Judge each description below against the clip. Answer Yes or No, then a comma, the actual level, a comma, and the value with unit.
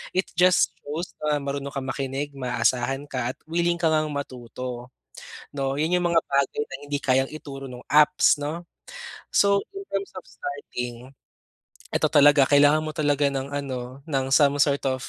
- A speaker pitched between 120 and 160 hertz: Yes, medium, 140 Hz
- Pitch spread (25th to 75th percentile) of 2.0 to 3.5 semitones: Yes, narrow, 2.5 semitones